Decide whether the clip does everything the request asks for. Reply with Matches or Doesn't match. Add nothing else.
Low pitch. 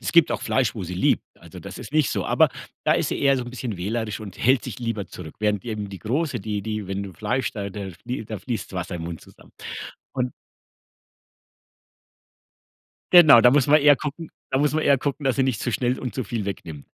Matches